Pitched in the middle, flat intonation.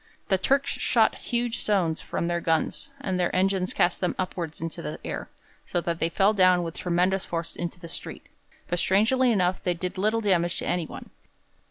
Yes: medium, 180 Hz; narrow, 2.3 semitones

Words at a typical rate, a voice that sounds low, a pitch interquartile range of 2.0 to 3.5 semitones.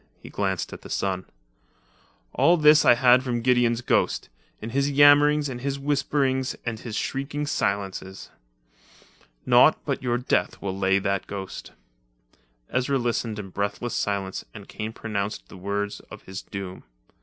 No: average, 150 wpm; low, 115 Hz; wide, 5.4 semitones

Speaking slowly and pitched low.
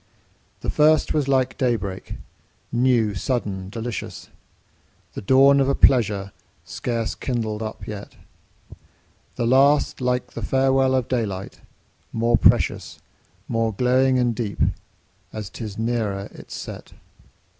Yes: slow, 125 wpm; low, 120 Hz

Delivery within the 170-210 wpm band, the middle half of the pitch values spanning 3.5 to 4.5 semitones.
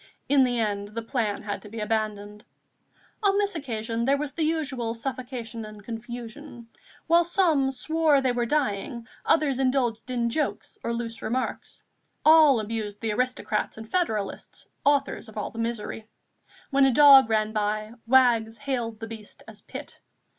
No: average, 160 wpm; average, 4.0 semitones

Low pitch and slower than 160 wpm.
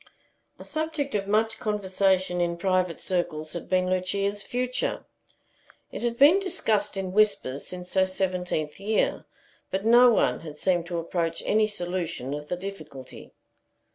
No: medium, 185 Hz; average, 145 wpm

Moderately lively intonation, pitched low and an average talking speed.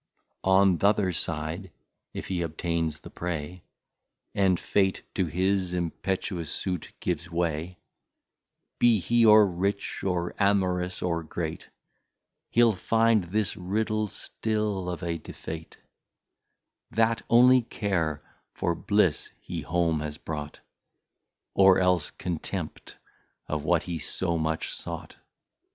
No: average, 3.3 semitones; very low, 90 Hz; slow, 115 wpm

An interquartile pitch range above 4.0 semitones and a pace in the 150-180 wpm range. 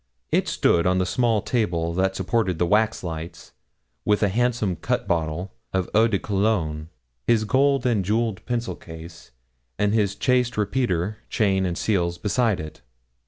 Yes: average, 4.5 semitones; average, 155 wpm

